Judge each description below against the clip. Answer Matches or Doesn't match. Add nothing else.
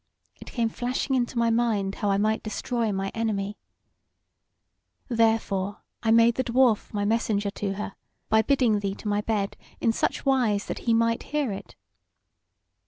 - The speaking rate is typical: Matches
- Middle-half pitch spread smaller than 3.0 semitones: Matches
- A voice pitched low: Doesn't match